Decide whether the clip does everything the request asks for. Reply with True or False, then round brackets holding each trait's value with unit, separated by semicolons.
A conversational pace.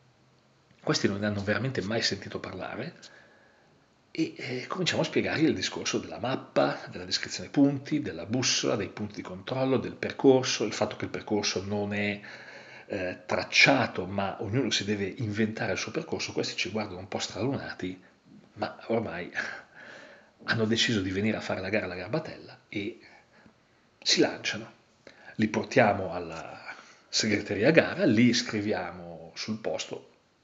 True (150 wpm)